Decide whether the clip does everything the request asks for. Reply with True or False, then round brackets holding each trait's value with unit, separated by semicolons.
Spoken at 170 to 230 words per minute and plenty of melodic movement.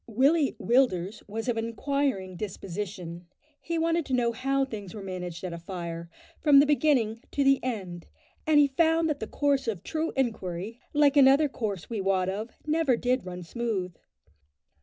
True (175 wpm; 6.9 semitones)